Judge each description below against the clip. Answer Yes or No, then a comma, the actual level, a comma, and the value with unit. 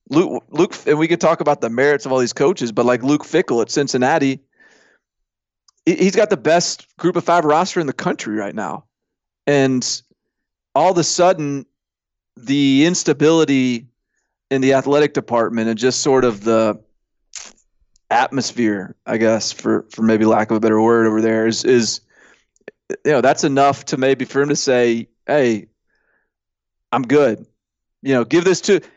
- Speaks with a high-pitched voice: No, low, 135 Hz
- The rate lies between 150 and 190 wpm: Yes, average, 170 wpm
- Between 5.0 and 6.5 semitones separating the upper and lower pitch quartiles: Yes, wide, 5.6 semitones